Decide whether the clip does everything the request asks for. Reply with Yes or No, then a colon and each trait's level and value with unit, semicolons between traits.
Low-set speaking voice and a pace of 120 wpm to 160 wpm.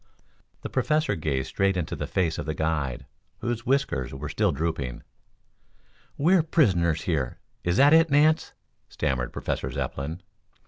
Yes: very low, 85 Hz; average, 150 wpm